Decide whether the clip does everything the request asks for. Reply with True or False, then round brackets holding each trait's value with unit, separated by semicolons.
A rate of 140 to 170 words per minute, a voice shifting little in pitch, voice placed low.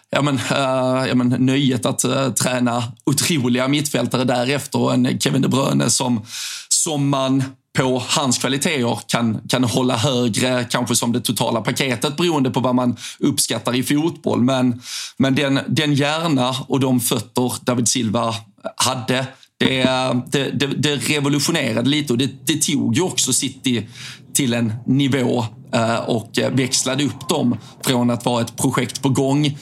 True (155 wpm; 2.0 semitones; 130 Hz)